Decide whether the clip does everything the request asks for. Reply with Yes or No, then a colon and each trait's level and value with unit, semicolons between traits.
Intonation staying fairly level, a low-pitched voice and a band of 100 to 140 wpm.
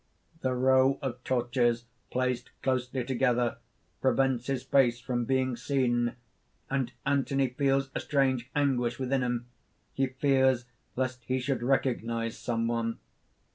Yes: narrow, 1.8 semitones; low, 130 Hz; slow, 135 wpm